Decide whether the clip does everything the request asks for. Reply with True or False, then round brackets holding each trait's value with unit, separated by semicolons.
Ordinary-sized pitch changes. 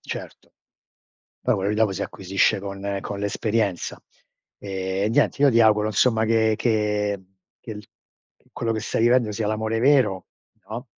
False (2.1 semitones)